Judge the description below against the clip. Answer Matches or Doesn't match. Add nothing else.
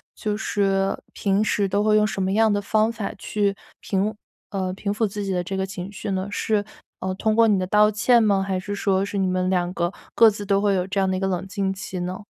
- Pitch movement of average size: Doesn't match